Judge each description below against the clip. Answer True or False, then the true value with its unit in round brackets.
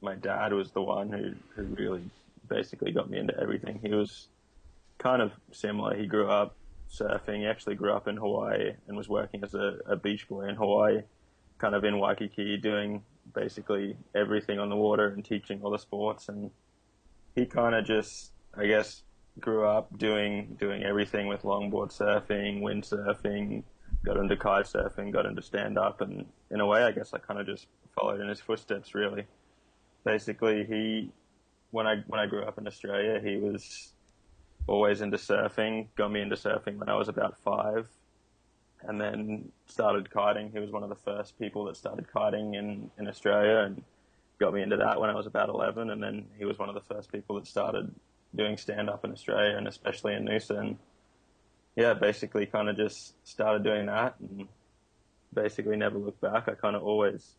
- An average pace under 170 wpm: False (185 wpm)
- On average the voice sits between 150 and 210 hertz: False (105 Hz)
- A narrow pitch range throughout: True (0.9 semitones)